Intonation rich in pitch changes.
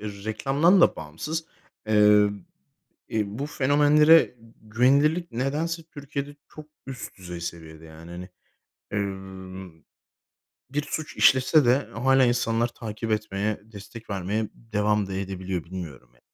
Yes: wide, 6.4 semitones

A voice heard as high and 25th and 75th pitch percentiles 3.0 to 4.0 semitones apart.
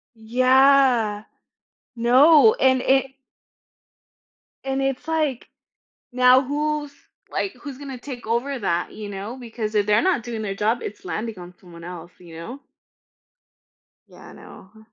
No: high, 245 Hz; average, 4.4 semitones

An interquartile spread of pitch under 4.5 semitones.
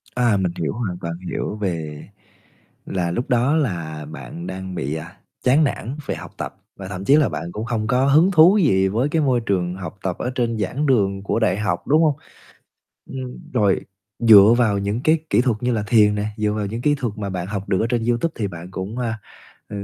No: average, 4.8 semitones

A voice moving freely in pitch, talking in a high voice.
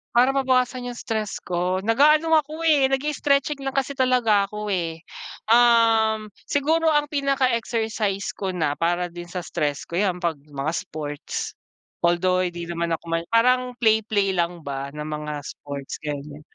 Yes: wide, 7.0 semitones; high, 210 Hz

